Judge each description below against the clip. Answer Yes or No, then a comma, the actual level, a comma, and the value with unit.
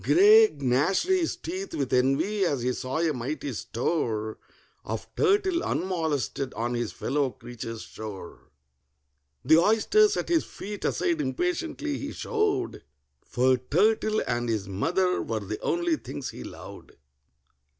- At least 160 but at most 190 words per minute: No, slow, 135 wpm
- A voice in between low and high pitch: Yes, medium, 165 Hz